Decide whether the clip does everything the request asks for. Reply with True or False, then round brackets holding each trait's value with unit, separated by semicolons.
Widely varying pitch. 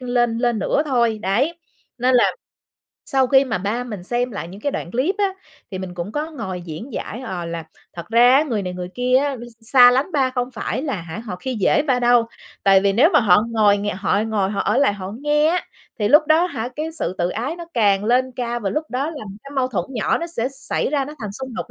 False (5.0 semitones)